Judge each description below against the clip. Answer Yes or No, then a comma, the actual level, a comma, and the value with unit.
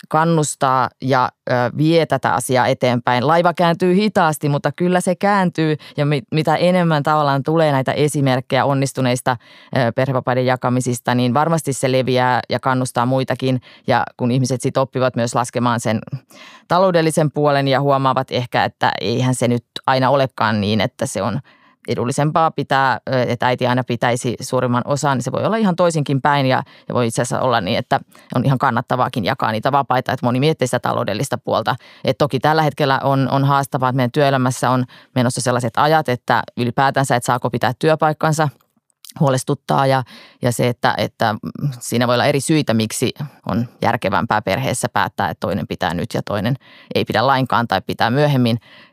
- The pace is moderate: No, fast, 165 wpm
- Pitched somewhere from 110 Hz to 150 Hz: Yes, low, 130 Hz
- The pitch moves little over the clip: No, average, 3.0 semitones